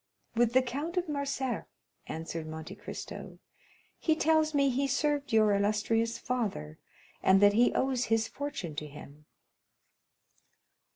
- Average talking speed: No, slow, 130 wpm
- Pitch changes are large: Yes, wide, 5.8 semitones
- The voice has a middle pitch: No, high, 240 Hz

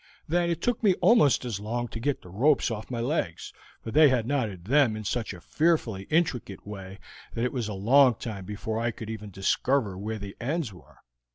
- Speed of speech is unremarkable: No, fast, 210 wpm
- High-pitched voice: No, low, 115 Hz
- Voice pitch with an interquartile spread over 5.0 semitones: Yes, wide, 5.4 semitones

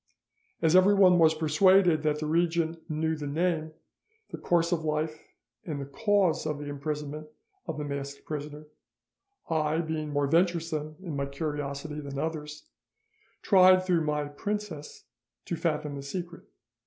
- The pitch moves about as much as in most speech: No, narrow, 2.3 semitones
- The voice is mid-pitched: Yes, medium, 155 Hz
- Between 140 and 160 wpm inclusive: Yes, average, 145 wpm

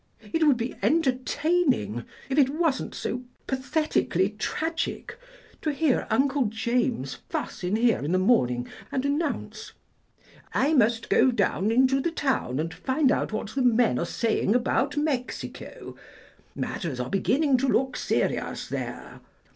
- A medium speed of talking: Yes, average, 145 wpm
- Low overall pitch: No, very high, 255 Hz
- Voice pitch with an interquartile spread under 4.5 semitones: No, average, 4.9 semitones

